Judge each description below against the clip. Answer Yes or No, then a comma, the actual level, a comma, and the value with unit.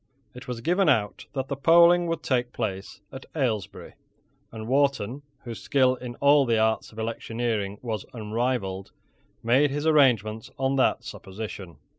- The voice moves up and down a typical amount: Yes, average, 4.0 semitones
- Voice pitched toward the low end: Yes, low, 120 Hz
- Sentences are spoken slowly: No, average, 150 wpm